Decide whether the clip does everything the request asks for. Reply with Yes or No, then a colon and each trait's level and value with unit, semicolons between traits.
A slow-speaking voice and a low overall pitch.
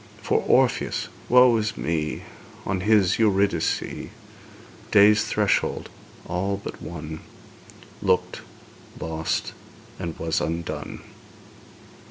Yes: slow, 90 wpm; very low, 95 Hz